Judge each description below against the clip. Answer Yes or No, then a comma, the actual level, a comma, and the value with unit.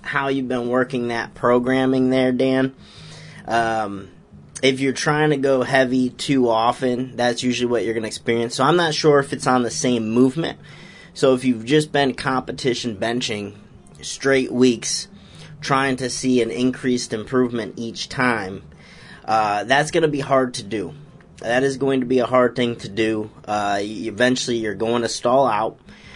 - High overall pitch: No, low, 125 Hz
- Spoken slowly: No, average, 175 wpm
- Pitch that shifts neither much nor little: No, narrow, 2.3 semitones